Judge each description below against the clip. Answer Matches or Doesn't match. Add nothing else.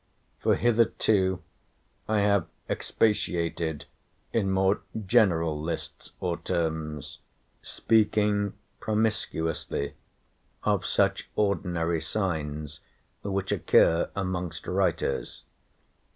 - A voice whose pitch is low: Matches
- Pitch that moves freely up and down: Doesn't match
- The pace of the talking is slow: Matches